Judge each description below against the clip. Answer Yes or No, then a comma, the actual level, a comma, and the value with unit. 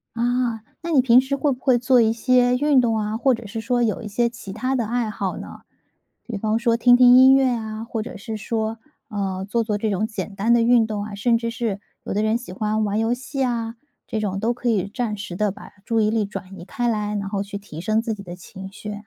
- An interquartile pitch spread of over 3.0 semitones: No, average, 2.7 semitones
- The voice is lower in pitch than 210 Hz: No, high, 225 Hz